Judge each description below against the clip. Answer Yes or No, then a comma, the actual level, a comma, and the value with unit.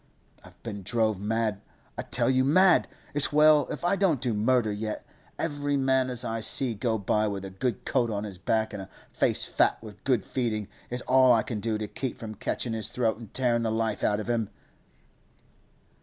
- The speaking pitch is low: Yes, low, 115 Hz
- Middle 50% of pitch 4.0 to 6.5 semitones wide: No, average, 3.3 semitones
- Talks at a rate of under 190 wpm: No, average, 200 wpm